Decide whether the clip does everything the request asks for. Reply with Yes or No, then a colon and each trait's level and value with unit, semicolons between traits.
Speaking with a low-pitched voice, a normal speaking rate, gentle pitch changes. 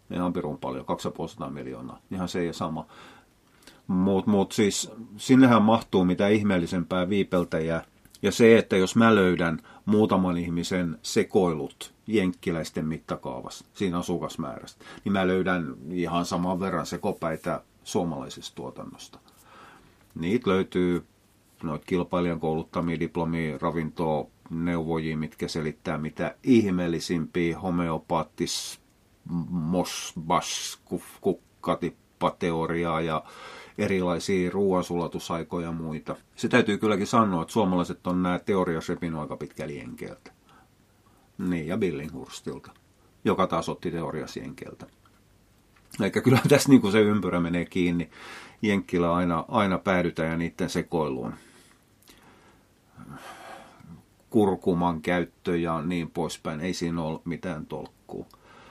Yes: very low, 90 Hz; average, 105 wpm; narrow, 2.3 semitones